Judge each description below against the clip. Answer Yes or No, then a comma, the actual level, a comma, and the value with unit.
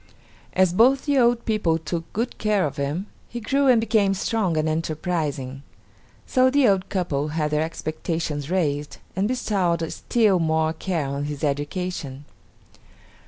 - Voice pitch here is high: No, medium, 170 Hz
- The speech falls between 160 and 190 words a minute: No, average, 150 wpm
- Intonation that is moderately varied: No, wide, 5.8 semitones